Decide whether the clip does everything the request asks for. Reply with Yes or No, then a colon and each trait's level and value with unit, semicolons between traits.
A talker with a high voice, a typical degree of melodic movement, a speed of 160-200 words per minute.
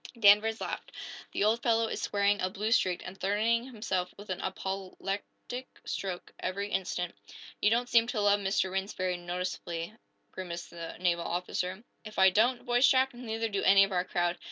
Yes: high, 195 Hz; average, 3.4 semitones; average, 180 wpm